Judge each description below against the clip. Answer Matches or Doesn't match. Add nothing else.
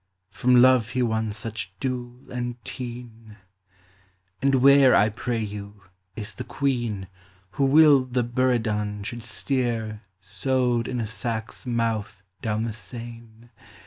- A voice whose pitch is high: Doesn't match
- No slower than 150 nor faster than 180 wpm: Doesn't match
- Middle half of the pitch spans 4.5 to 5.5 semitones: Doesn't match